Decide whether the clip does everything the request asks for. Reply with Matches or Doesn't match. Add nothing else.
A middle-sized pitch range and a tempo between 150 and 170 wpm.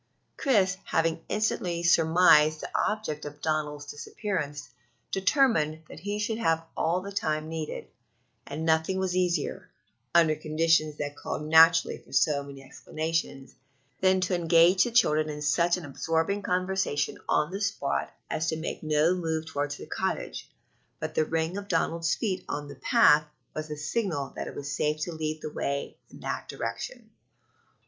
Matches